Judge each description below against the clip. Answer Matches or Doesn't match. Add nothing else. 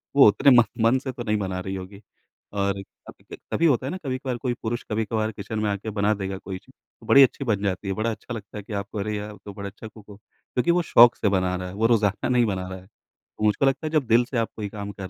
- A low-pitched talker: Matches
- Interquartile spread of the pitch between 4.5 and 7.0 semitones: Doesn't match